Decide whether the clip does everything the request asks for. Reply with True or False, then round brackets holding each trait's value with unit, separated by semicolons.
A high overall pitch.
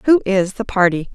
True (205 Hz)